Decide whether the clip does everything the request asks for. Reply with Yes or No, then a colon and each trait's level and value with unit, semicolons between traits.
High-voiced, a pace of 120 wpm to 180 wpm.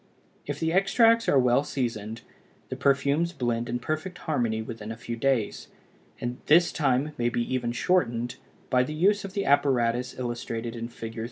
No: low, 125 Hz; average, 170 wpm